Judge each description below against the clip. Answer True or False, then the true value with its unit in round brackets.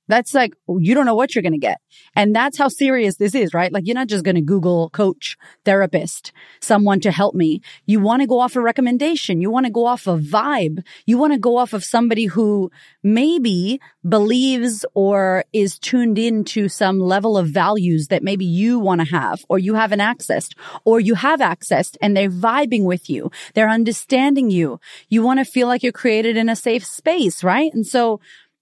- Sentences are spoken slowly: False (205 wpm)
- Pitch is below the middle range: False (215 Hz)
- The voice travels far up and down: False (4.4 semitones)